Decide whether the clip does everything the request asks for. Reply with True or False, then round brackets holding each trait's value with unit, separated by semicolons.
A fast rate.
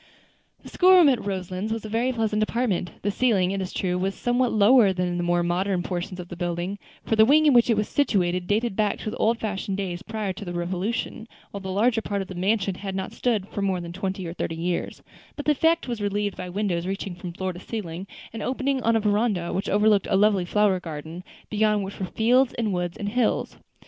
True (235 wpm)